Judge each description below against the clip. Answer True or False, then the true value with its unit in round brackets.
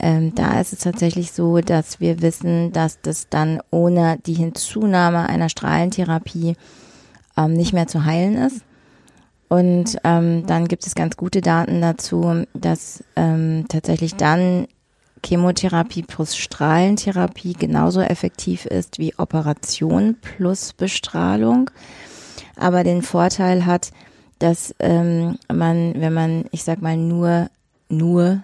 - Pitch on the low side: False (170 Hz)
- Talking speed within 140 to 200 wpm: False (125 wpm)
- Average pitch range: False (1.7 semitones)